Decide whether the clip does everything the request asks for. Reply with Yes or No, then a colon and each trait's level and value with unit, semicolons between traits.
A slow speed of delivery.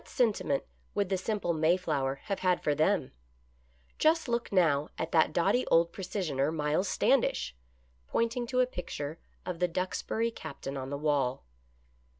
No: average, 155 wpm